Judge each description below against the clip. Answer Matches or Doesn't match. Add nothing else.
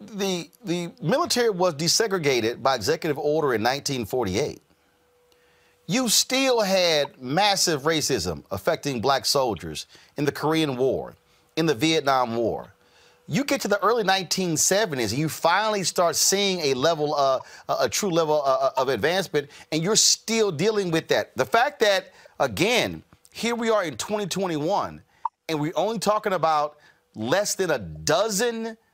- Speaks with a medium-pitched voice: Matches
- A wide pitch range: Matches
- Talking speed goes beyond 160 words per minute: Doesn't match